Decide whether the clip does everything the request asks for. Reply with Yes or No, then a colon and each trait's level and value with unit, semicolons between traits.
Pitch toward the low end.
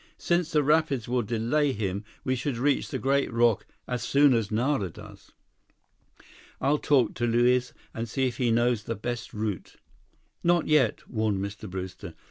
Yes: low, 120 Hz